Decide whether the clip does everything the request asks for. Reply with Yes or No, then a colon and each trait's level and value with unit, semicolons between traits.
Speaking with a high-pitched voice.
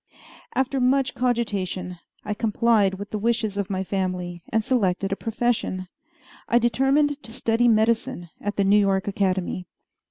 Yes: high, 210 Hz